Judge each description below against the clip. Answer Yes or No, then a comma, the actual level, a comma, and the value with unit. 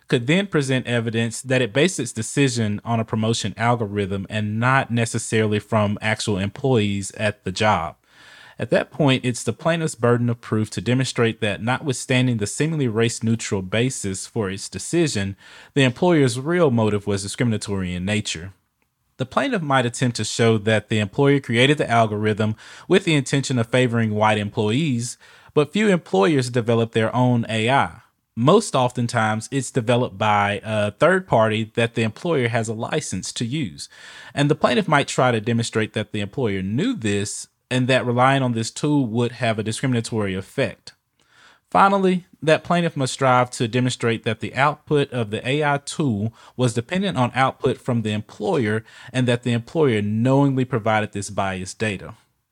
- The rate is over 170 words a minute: No, average, 165 wpm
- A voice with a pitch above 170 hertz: No, low, 120 Hz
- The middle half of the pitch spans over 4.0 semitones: No, average, 3.6 semitones